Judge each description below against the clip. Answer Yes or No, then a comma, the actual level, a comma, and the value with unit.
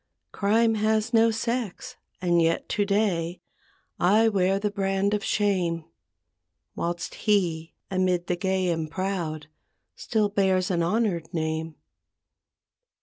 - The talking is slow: Yes, slow, 120 wpm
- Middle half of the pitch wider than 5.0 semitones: No, average, 3.6 semitones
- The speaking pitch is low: No, high, 190 Hz